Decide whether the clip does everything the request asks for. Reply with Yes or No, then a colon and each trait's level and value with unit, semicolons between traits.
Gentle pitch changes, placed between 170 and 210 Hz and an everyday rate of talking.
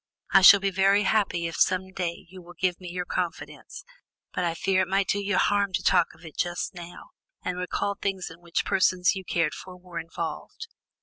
No: narrow, 1.9 semitones; medium, 185 Hz; fast, 210 wpm